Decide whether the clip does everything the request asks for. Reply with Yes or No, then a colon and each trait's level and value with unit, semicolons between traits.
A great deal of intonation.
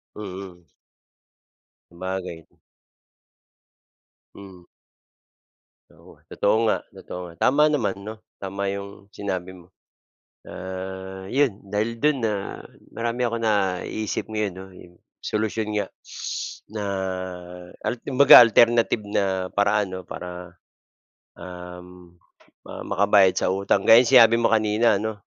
No: average, 3.1 semitones